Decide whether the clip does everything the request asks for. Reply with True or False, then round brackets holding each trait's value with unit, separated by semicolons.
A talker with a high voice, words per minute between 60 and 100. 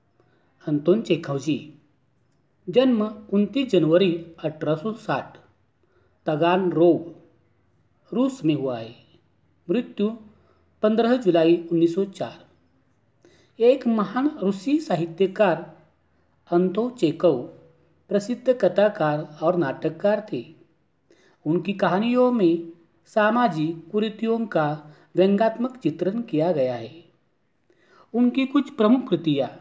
False (175 Hz; 95 wpm)